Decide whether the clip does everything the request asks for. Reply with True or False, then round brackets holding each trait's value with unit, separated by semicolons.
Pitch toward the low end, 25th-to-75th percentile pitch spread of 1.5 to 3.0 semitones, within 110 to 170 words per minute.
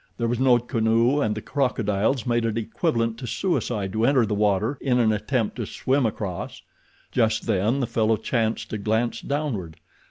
False (115 Hz; 2.6 semitones; 180 wpm)